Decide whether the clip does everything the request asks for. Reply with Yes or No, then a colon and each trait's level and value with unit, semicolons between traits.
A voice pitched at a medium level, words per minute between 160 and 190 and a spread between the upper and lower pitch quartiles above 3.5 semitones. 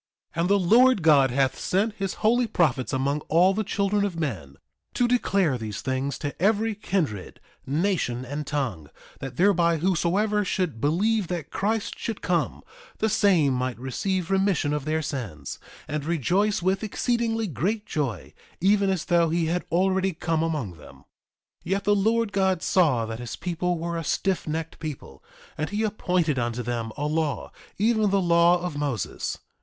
Yes: medium, 170 Hz; average, 170 wpm; wide, 5.6 semitones